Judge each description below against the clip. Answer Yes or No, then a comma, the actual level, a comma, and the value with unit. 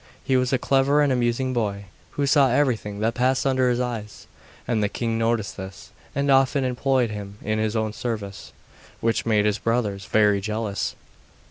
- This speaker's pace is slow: No, average, 175 wpm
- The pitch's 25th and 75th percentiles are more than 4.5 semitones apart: No, average, 3.6 semitones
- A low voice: Yes, low, 115 Hz